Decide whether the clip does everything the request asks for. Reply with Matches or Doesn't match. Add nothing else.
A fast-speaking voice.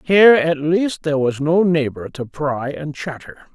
Doesn't match